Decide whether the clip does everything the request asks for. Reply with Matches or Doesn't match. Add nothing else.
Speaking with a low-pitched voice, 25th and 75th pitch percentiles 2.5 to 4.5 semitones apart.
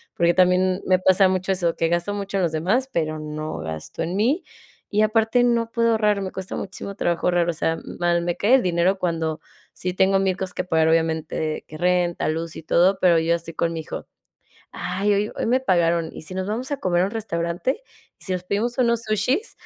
Doesn't match